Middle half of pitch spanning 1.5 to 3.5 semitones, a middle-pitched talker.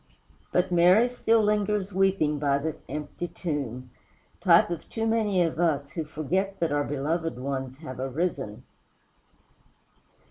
No: average, 5.2 semitones; medium, 165 Hz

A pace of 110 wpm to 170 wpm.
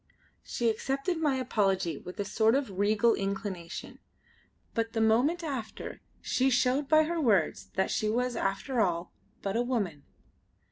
Yes: average, 145 wpm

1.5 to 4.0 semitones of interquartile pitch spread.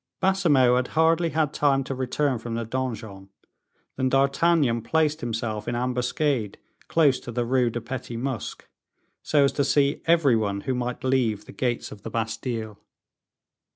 Yes: average, 3.4 semitones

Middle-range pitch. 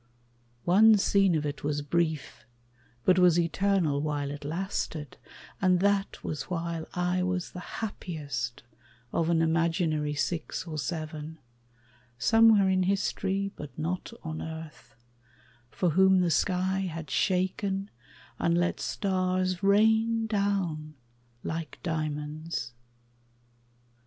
Yes: medium, 175 Hz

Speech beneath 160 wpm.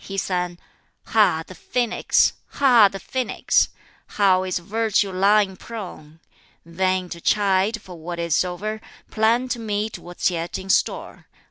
Yes: average, 140 wpm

